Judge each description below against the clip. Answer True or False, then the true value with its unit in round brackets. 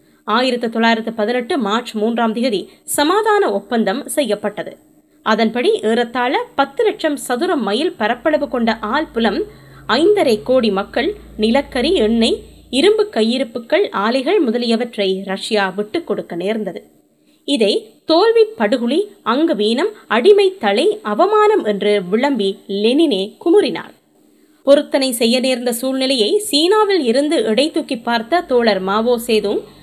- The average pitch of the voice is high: True (250 Hz)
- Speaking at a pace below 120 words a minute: True (110 wpm)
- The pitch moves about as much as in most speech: False (7.0 semitones)